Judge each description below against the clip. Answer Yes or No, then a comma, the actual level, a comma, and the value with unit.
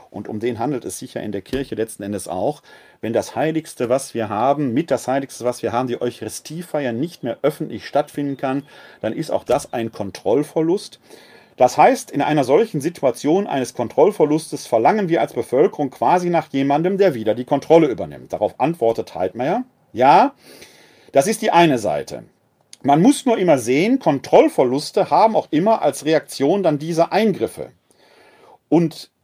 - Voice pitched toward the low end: No, medium, 145 Hz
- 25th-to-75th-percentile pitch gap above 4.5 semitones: Yes, wide, 5.5 semitones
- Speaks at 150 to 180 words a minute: Yes, average, 170 wpm